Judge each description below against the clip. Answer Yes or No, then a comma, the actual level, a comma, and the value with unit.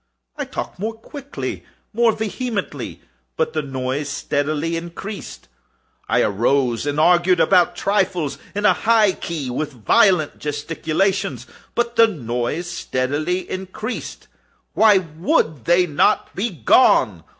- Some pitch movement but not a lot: No, wide, 6.2 semitones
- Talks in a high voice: No, medium, 175 Hz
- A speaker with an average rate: No, slow, 120 wpm